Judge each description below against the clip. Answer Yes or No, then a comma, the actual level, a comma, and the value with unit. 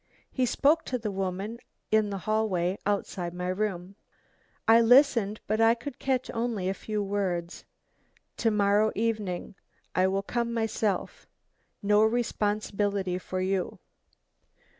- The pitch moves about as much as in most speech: Yes, average, 3.0 semitones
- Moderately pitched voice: No, high, 210 Hz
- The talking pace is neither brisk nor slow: No, slow, 130 wpm